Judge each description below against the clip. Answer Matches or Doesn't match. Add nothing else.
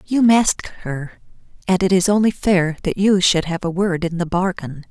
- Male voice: Doesn't match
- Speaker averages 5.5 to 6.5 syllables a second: Doesn't match